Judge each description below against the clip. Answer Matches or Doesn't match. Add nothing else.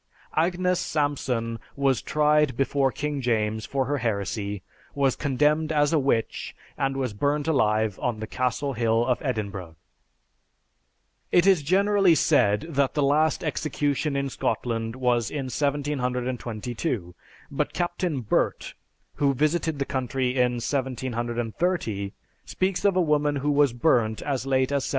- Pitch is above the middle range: Doesn't match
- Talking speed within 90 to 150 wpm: Matches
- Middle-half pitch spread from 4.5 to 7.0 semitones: Doesn't match